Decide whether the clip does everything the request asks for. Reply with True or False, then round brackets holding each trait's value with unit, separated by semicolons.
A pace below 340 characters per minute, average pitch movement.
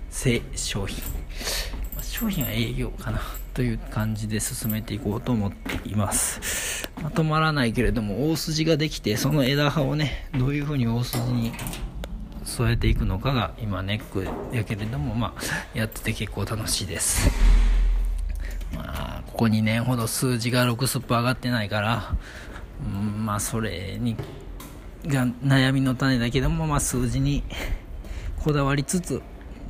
True (285 characters per minute; 4.4 semitones)